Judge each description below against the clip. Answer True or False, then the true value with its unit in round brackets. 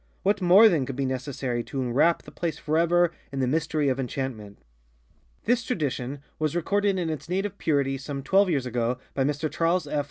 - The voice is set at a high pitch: False (150 Hz)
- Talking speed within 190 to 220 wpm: True (195 wpm)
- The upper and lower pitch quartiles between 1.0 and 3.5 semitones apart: False (4.6 semitones)